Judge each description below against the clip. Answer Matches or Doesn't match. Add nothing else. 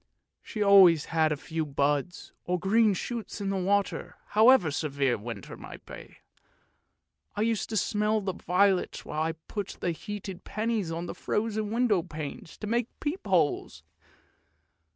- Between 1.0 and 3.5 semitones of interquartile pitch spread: Doesn't match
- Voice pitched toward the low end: Doesn't match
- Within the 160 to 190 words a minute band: Doesn't match